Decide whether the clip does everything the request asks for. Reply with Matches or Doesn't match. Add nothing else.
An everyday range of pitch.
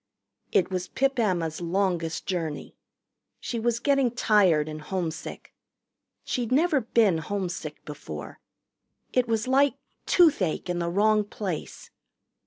Doesn't match